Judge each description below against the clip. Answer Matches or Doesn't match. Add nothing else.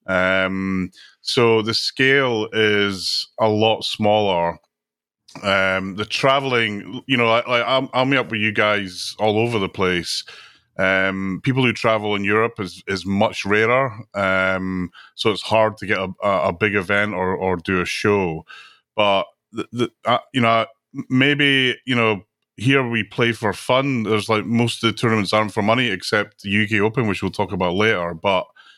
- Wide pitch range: Doesn't match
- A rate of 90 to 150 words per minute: Doesn't match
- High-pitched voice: Doesn't match